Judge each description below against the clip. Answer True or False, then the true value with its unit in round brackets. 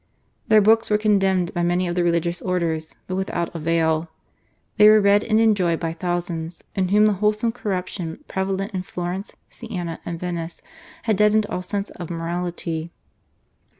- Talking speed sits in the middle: True (160 wpm)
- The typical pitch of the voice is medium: True (180 Hz)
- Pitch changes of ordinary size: True (3.4 semitones)